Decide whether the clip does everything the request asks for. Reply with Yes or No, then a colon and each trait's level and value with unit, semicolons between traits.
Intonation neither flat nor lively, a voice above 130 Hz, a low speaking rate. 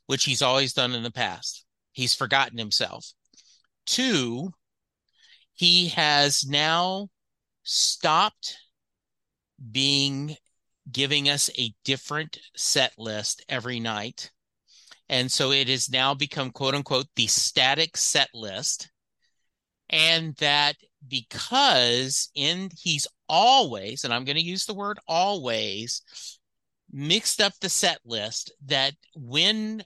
Yes: average, 4.1 semitones; medium, 140 Hz; slow, 115 wpm